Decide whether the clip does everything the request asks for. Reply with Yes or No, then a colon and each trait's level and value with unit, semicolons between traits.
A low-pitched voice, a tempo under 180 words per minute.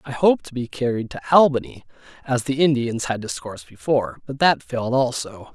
No: low, 130 Hz; average, 185 wpm